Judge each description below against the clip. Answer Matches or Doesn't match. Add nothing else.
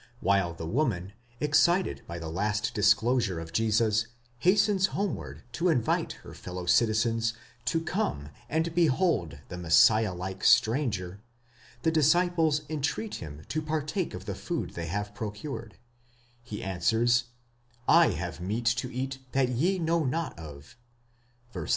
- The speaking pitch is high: Doesn't match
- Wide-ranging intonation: Matches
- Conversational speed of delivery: Matches